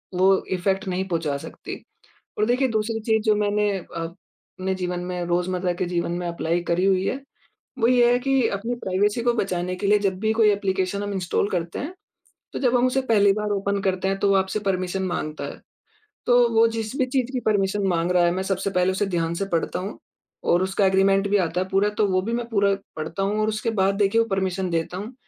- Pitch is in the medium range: No, high, 195 Hz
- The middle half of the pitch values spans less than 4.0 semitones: Yes, average, 2.8 semitones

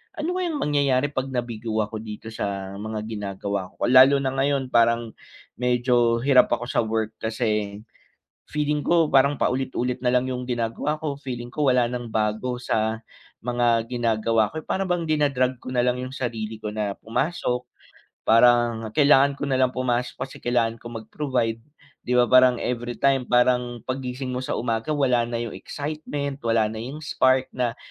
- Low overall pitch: Yes, low, 125 Hz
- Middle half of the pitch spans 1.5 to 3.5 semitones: Yes, average, 2.7 semitones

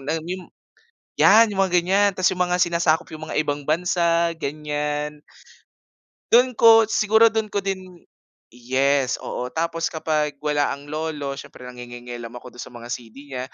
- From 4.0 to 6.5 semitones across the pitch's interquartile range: Yes, average, 4.6 semitones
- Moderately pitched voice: Yes, medium, 155 Hz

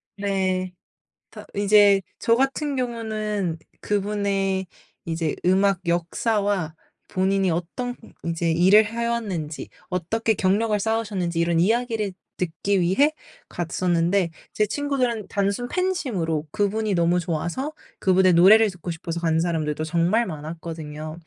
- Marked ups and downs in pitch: No, average, 4.2 semitones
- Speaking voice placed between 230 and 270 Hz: No, high, 190 Hz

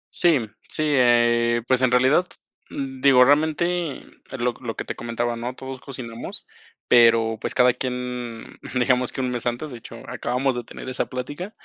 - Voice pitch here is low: Yes, low, 125 Hz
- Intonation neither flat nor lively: No, narrow, 2.1 semitones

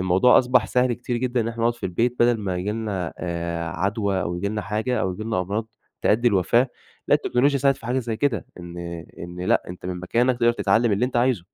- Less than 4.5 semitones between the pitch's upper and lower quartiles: No, average, 4.9 semitones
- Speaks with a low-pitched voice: Yes, low, 110 Hz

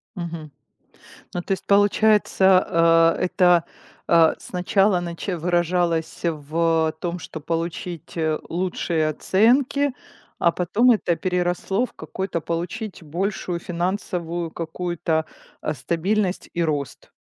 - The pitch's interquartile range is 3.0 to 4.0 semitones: No, narrow, 2.4 semitones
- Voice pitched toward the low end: No, medium, 175 Hz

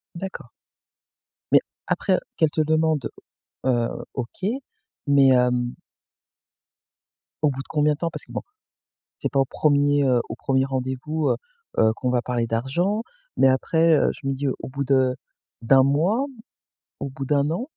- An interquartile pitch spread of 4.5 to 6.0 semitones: No, average, 3.2 semitones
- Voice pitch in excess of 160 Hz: No, medium, 140 Hz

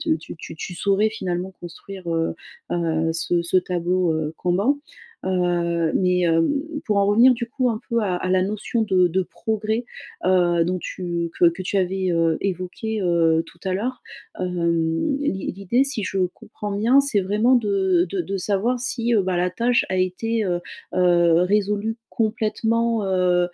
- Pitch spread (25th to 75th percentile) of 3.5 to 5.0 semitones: Yes, average, 3.8 semitones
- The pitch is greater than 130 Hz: Yes, medium, 185 Hz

